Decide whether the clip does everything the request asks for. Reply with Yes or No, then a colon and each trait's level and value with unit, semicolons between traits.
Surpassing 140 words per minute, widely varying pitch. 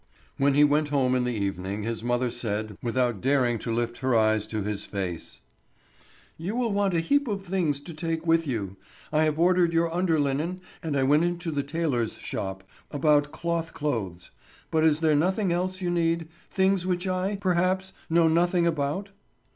Yes: average, 180 wpm; wide, 6.2 semitones